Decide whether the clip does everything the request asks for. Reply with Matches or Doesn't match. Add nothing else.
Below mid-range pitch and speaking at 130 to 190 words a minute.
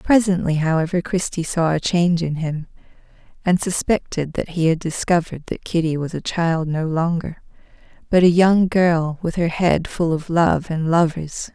Doesn't match